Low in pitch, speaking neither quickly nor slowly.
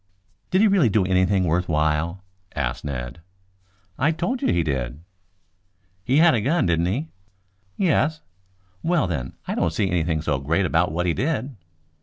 Yes: very low, 90 Hz; average, 170 wpm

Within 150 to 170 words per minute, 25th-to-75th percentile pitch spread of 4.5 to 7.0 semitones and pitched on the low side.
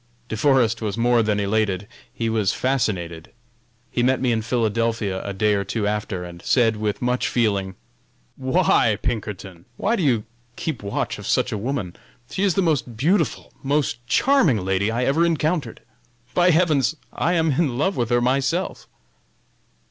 Yes: average, 165 wpm; average, 5.1 semitones; low, 120 Hz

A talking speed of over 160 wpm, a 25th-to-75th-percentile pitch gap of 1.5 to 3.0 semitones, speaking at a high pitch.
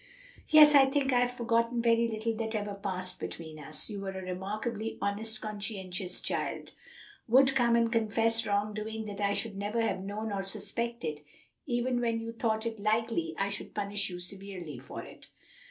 Yes: average, 180 wpm; average, 2.7 semitones; high, 215 Hz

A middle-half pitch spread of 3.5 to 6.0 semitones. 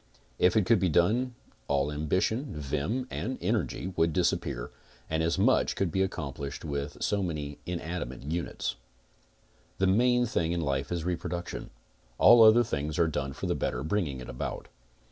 Yes: average, 5.2 semitones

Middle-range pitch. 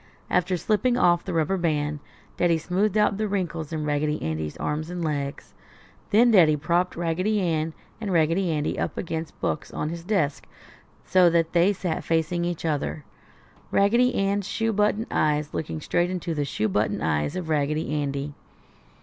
Yes: medium, 165 Hz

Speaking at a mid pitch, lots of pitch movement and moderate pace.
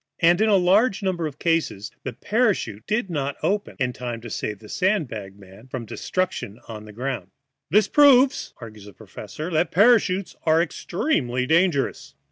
Yes: medium, 160 Hz; wide, 8.9 semitones; average, 170 wpm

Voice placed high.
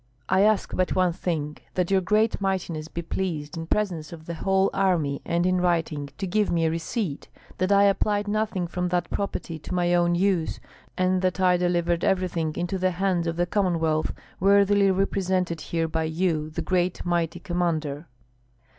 No: medium, 175 Hz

